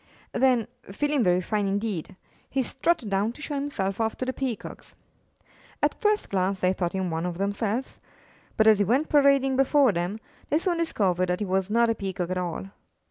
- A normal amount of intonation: No, wide, 6.0 semitones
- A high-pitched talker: Yes, high, 215 Hz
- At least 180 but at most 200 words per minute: Yes, average, 190 wpm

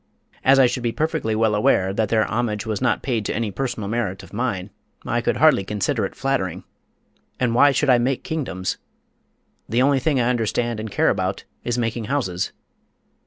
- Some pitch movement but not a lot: Yes, average, 3.4 semitones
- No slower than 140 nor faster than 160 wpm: No, average, 190 wpm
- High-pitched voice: No, low, 115 Hz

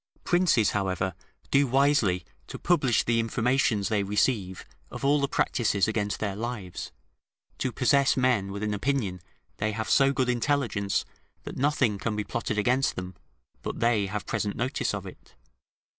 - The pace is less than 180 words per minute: Yes, average, 160 wpm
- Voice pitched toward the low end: Yes, low, 115 Hz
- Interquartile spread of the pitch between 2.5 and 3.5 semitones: No, average, 4.5 semitones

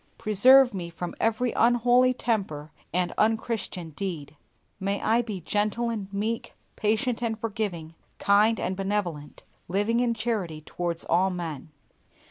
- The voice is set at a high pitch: Yes, high, 205 Hz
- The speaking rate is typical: No, slow, 130 wpm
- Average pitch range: Yes, average, 4.5 semitones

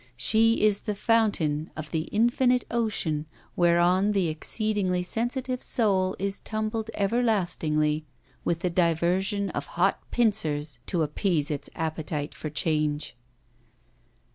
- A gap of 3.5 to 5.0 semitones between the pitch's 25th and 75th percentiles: No, wide, 5.6 semitones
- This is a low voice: No, medium, 185 Hz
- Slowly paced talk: Yes, slow, 115 wpm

